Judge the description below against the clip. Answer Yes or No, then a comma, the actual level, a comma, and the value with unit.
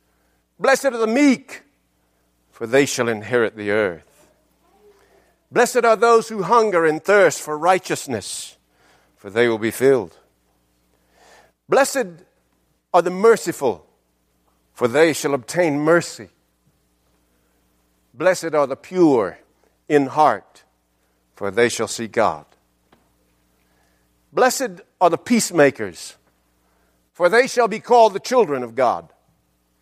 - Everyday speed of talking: No, slow, 115 wpm